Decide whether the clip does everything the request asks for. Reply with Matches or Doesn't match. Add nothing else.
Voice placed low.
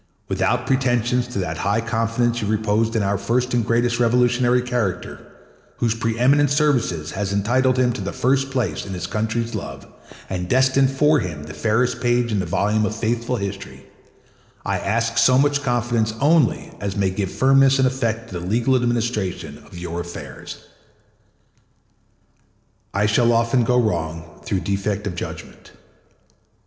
Matches